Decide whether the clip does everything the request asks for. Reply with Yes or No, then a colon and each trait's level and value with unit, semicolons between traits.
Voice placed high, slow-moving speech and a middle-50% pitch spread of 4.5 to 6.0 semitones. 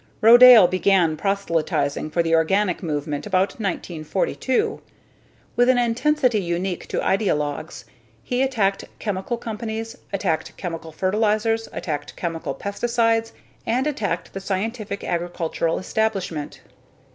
Yes: high, 195 Hz; slow, 110 wpm; average, 5.2 semitones